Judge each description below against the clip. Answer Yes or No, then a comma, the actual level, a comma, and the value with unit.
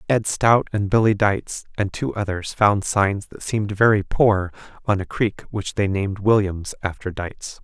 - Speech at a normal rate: Yes, average, 180 wpm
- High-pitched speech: No, low, 100 Hz